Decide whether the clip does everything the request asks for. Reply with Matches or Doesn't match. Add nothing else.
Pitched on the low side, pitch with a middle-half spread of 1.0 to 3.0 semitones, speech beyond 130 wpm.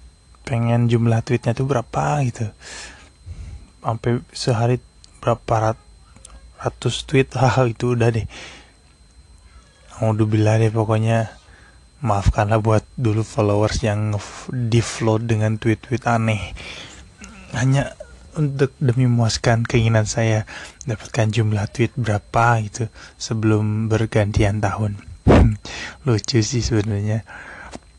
Doesn't match